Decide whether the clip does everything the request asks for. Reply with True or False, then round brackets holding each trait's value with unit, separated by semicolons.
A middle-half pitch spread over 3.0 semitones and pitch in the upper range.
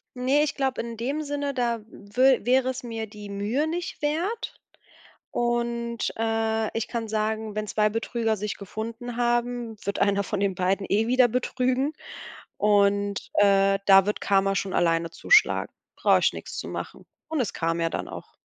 True (3.7 semitones; 225 Hz)